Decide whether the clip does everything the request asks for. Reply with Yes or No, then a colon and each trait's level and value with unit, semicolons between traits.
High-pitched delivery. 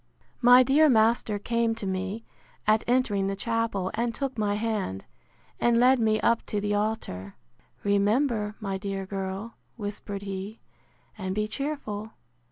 Yes: high, 215 Hz